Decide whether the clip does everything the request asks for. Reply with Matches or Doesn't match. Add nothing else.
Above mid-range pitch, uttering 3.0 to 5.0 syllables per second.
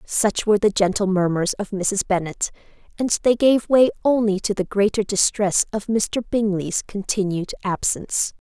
Matches